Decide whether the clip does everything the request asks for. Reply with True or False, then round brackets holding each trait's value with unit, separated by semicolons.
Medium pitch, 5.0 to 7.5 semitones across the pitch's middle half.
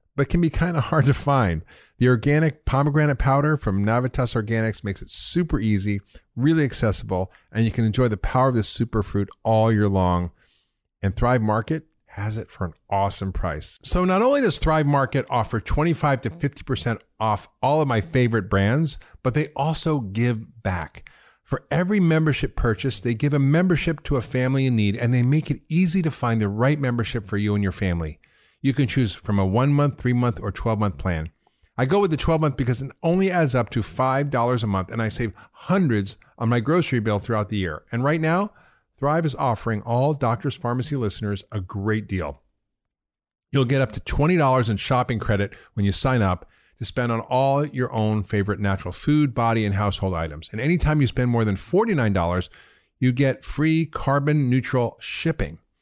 False (120 Hz; 5.5 semitones)